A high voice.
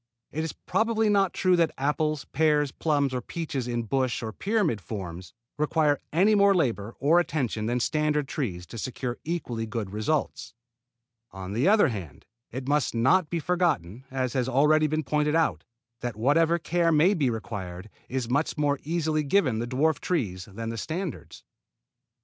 No: medium, 140 Hz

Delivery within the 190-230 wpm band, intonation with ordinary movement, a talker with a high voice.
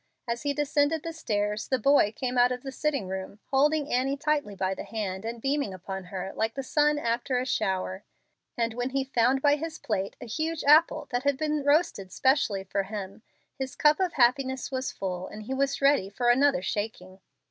No: average, 200 wpm; wide, 5.7 semitones; very high, 255 Hz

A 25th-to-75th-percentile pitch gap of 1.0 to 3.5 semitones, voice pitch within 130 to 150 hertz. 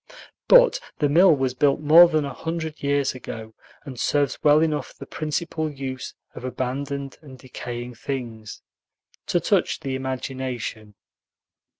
Yes: average, 3.0 semitones; low, 135 Hz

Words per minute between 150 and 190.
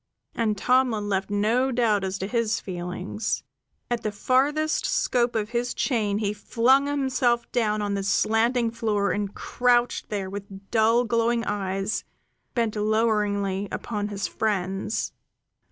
No: slow, 135 wpm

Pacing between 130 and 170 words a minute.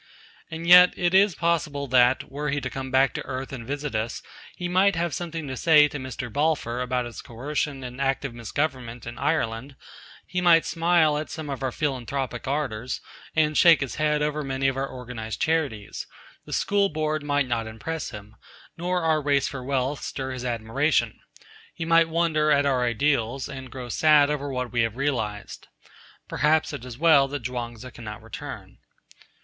No: average, 185 wpm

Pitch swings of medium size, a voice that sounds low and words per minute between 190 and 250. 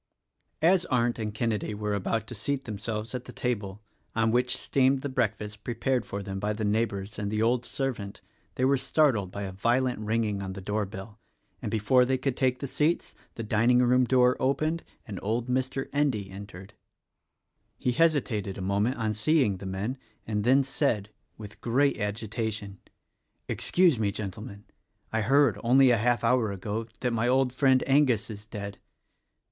No: average, 3.8 semitones; low, 115 Hz; average, 175 wpm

